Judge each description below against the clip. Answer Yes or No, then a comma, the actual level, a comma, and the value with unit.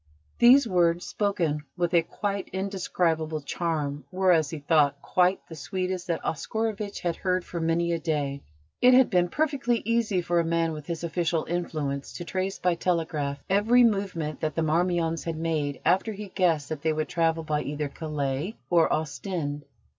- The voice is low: No, medium, 170 Hz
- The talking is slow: No, average, 175 wpm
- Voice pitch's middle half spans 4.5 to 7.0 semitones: No, average, 3.3 semitones